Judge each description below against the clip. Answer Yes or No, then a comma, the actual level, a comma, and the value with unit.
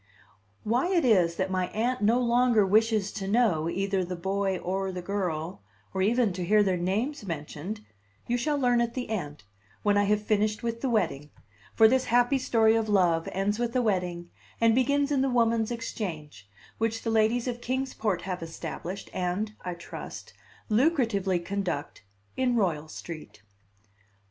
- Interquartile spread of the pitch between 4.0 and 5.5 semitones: Yes, average, 4.6 semitones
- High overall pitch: Yes, high, 210 Hz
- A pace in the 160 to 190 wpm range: Yes, average, 170 wpm